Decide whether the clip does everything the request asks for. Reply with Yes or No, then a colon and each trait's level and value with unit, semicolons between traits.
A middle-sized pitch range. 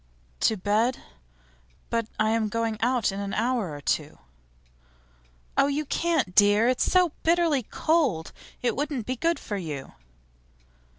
No: wide, 5.7 semitones